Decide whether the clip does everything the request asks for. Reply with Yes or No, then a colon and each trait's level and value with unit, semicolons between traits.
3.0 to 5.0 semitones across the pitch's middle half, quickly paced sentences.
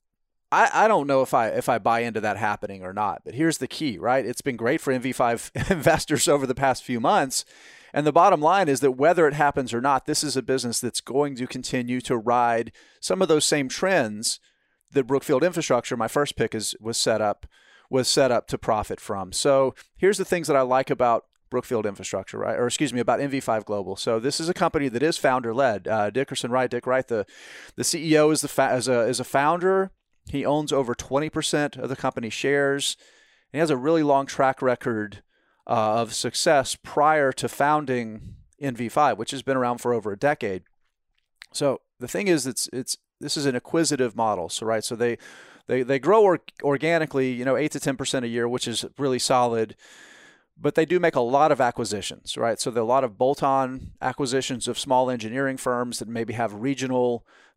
Yes: average, 3.3 semitones; fast, 210 wpm